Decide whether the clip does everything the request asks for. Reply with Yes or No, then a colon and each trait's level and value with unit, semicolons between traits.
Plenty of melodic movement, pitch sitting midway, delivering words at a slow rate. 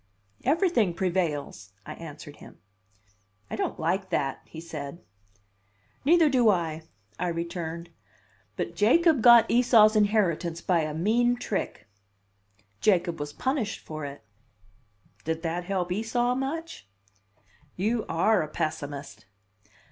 Yes: wide, 6.1 semitones; medium, 180 Hz; slow, 120 wpm